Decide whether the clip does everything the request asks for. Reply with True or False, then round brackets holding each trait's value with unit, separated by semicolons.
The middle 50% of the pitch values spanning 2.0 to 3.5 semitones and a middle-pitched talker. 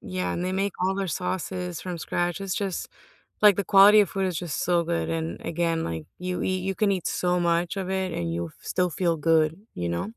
True (2.9 semitones; 180 Hz)